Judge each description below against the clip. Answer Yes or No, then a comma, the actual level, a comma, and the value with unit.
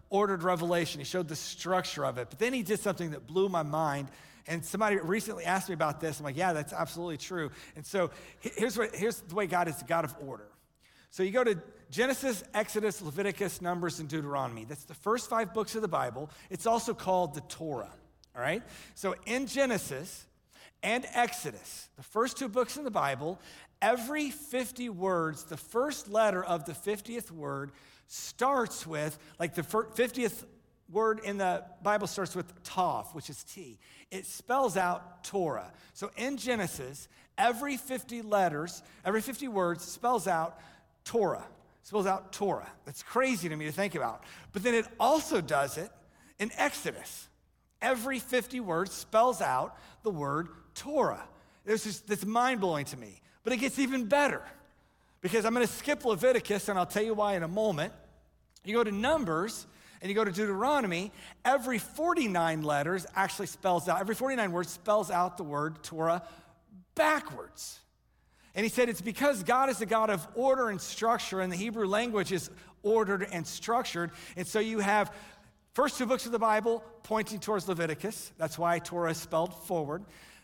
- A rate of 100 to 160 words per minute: No, average, 175 wpm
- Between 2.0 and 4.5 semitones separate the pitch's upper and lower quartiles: No, average, 5.3 semitones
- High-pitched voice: Yes, high, 200 Hz